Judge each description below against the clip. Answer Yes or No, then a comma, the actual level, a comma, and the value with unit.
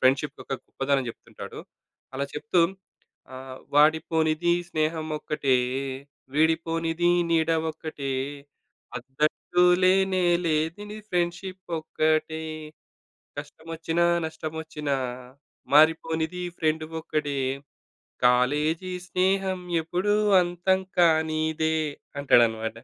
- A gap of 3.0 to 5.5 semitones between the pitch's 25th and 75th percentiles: No, narrow, 2.4 semitones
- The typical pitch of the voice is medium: Yes, medium, 160 Hz